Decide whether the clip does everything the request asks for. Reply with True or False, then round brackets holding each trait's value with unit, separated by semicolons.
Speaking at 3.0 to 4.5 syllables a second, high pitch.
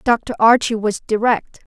True (4.2 syllables/s; 225 Hz)